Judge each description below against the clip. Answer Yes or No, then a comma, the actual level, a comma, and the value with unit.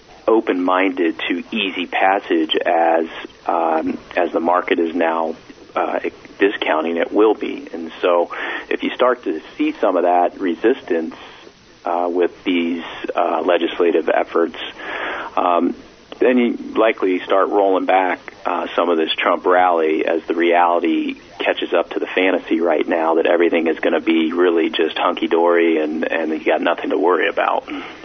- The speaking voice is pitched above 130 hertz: No, very low, 95 Hz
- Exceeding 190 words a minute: No, average, 155 wpm